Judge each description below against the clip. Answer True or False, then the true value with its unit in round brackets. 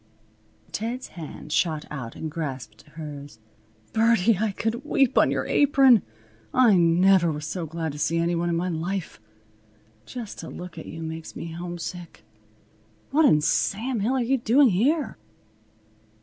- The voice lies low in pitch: False (175 Hz)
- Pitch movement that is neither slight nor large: False (6.2 semitones)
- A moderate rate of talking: True (155 wpm)